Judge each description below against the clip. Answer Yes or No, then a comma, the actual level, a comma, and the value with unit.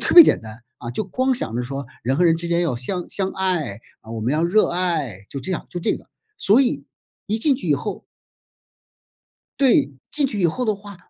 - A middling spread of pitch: No, wide, 7.9 semitones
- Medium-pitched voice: Yes, medium, 175 Hz